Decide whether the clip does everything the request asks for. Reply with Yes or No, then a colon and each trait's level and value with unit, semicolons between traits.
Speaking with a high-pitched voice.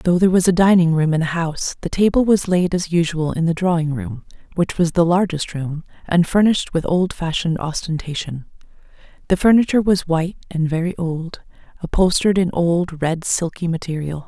No: medium, 170 Hz